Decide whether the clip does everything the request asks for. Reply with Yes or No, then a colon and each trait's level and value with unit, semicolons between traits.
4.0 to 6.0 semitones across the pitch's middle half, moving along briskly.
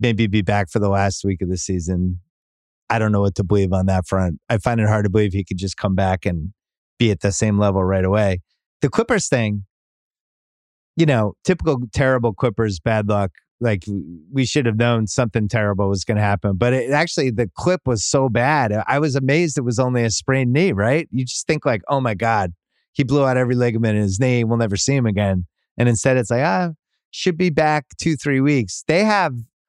Yes: average, 5.0 semitones; fast, 220 wpm